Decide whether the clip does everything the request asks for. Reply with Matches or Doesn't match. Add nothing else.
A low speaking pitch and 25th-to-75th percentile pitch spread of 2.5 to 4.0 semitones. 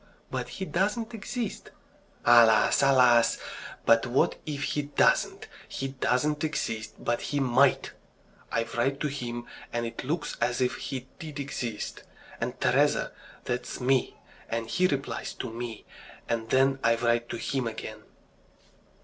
Matches